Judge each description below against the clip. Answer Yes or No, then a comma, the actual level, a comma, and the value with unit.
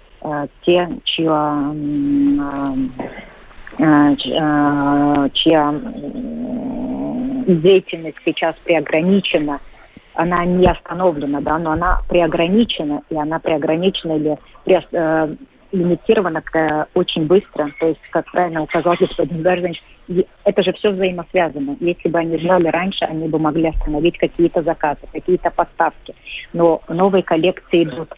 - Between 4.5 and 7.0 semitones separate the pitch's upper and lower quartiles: No, average, 3.0 semitones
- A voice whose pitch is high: No, medium, 165 Hz